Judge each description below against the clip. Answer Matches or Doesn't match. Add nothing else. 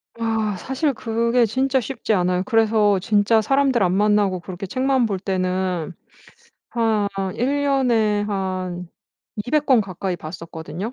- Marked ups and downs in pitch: Doesn't match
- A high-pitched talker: Matches